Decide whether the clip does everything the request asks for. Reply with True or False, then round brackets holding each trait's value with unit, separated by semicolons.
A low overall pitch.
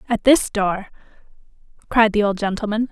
False (210 Hz)